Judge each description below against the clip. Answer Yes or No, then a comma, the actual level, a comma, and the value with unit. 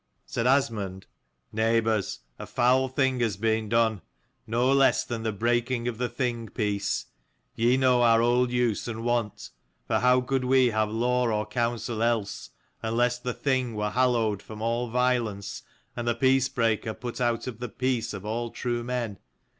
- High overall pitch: No, low, 120 Hz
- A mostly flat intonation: Yes, narrow, 2.0 semitones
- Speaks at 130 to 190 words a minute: Yes, average, 175 wpm